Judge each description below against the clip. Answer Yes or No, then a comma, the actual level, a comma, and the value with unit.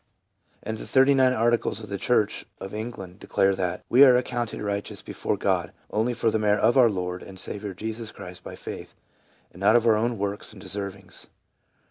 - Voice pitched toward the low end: Yes, low, 105 Hz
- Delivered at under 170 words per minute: No, average, 195 wpm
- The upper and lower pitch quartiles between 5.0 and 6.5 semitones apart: No, average, 3.4 semitones